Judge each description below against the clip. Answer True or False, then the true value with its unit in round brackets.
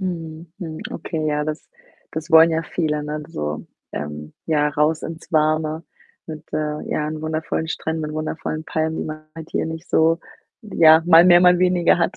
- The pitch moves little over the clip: True (1.2 semitones)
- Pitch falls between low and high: True (160 Hz)